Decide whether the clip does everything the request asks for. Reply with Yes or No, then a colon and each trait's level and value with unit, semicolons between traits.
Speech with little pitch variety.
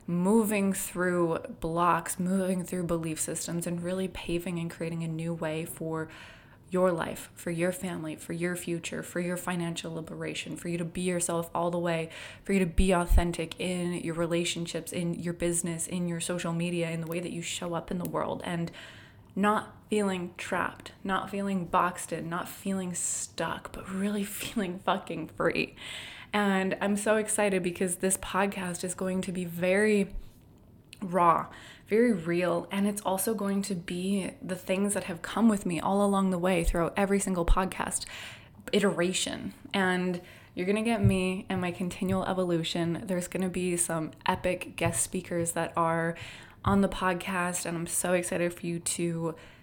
Yes: narrow, 1.9 semitones